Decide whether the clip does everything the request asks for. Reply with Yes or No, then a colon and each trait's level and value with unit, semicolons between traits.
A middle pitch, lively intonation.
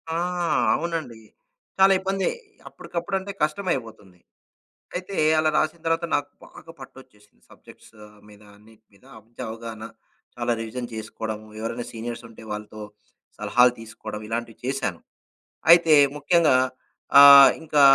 No: low, 120 Hz; wide, 6.4 semitones